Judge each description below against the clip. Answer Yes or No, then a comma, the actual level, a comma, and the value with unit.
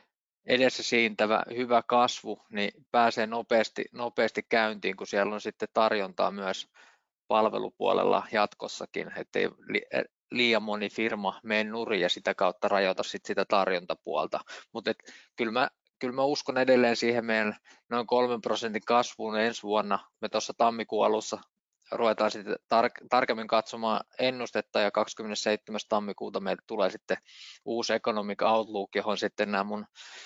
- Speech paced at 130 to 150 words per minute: Yes, average, 135 wpm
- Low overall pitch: Yes, low, 110 Hz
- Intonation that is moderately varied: No, narrow, 1.8 semitones